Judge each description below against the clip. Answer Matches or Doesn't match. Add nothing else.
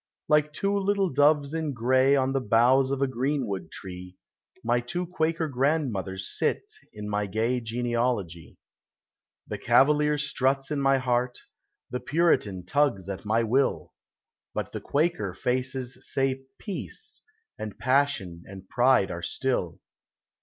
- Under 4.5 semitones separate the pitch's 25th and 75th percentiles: Doesn't match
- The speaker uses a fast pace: Doesn't match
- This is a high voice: Doesn't match